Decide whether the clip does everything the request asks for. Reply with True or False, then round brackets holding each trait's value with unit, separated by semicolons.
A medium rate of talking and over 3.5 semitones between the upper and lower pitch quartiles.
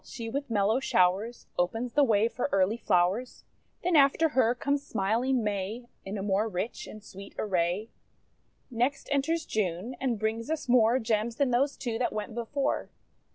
True (165 wpm; 3.9 semitones)